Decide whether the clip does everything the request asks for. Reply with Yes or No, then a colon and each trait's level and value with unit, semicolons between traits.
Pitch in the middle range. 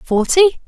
No: very high, 305 Hz